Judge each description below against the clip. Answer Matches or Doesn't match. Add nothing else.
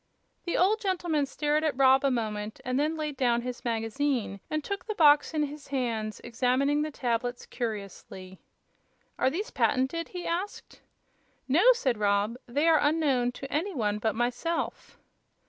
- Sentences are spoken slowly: Doesn't match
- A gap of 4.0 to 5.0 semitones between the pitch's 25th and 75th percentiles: Matches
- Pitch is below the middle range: Doesn't match